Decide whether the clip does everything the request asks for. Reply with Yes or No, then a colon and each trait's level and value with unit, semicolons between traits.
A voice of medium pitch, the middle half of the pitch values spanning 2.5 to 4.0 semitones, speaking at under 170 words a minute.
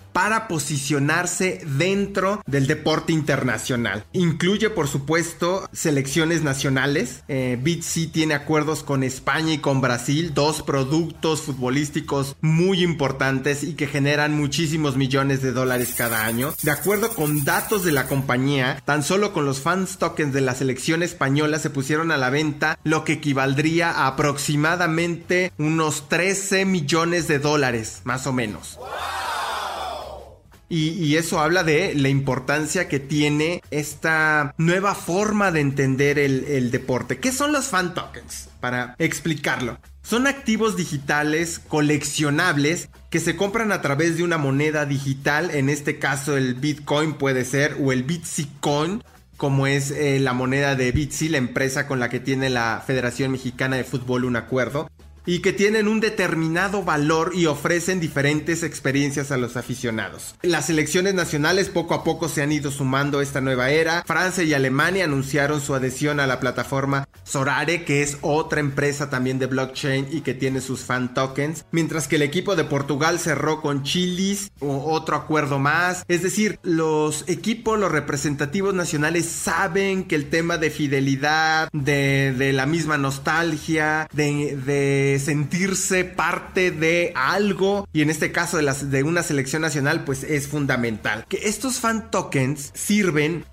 Yes: medium, 150 Hz; average, 3.4 semitones; average, 155 wpm